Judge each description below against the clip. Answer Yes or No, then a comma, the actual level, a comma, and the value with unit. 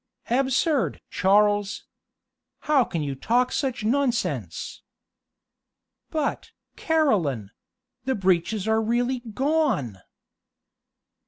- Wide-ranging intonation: Yes, wide, 5.7 semitones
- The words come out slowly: Yes, slow, 80 wpm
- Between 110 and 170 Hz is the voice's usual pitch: No, high, 235 Hz